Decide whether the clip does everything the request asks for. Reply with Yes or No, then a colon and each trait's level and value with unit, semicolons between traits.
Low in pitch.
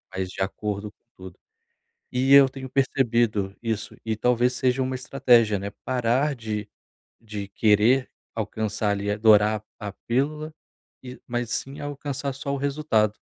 Yes: low, 120 Hz